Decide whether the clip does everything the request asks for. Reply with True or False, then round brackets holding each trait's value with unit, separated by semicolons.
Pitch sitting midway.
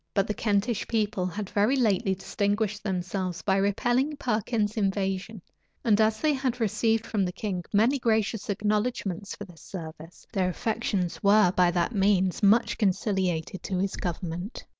False (205 Hz)